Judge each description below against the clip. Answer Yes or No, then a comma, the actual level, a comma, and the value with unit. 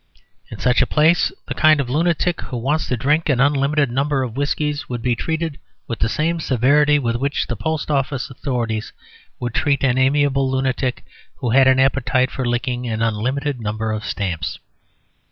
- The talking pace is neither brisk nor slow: Yes, average, 180 wpm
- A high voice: No, low, 130 Hz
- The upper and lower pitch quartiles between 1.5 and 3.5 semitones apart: Yes, average, 3.2 semitones